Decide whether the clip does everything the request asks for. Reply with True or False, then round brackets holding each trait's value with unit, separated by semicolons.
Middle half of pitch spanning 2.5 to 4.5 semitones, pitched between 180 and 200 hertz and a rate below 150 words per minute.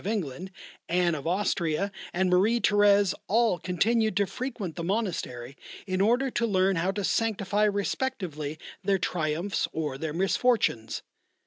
True (3.9 semitones; 190 Hz; 140 wpm)